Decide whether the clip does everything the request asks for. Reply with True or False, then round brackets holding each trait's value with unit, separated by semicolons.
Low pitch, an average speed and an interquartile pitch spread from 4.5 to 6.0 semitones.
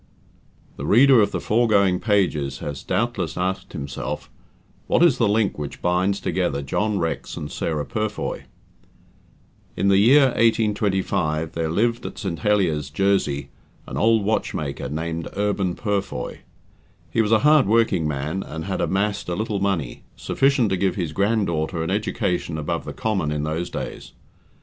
True (95 Hz; 155 wpm; 5.0 semitones)